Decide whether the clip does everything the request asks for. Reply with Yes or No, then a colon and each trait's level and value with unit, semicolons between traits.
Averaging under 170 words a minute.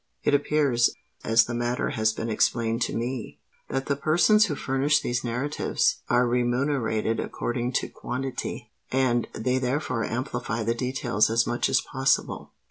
Yes: average, 140 wpm